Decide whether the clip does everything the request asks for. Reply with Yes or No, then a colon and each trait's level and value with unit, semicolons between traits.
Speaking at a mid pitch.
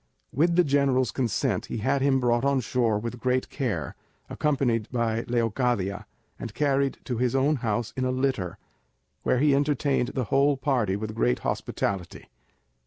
No: low, 125 Hz